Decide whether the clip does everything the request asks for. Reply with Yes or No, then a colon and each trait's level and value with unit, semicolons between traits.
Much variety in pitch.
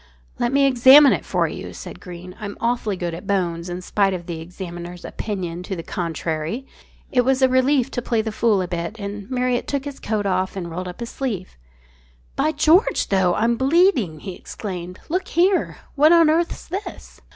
Yes: wide, 6.8 semitones